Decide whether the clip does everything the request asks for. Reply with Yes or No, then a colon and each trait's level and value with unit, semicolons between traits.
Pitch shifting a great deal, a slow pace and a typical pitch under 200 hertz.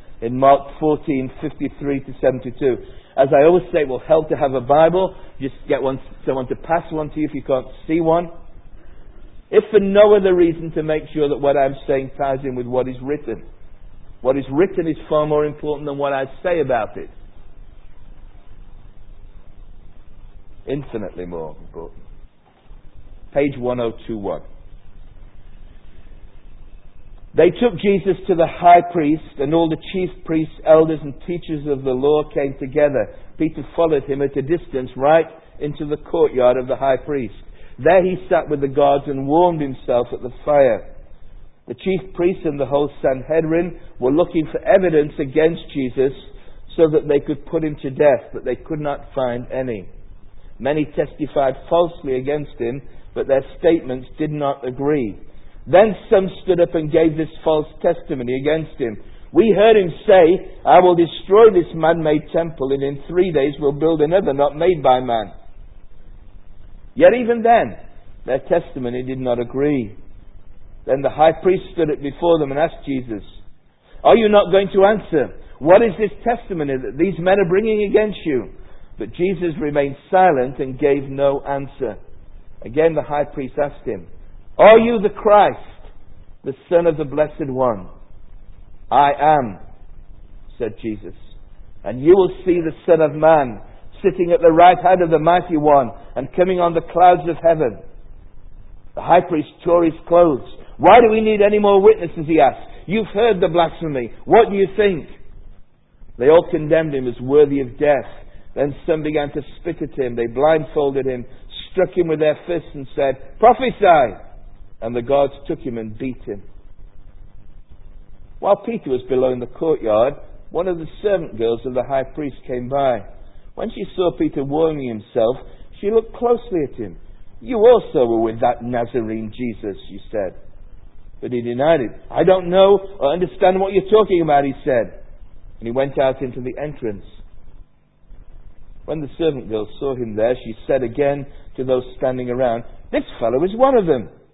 No: wide, 6.3 semitones; average, 170 wpm; medium, 140 Hz